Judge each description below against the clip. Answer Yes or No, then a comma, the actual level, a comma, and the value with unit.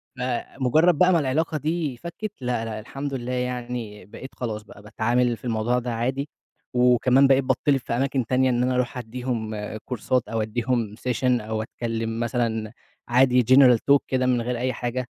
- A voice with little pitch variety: Yes, narrow, 2.1 semitones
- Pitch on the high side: No, low, 125 Hz